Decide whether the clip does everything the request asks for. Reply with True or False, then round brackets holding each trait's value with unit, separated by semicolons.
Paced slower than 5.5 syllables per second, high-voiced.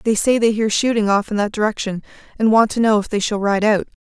False (6.1 syllables/s; 210 Hz)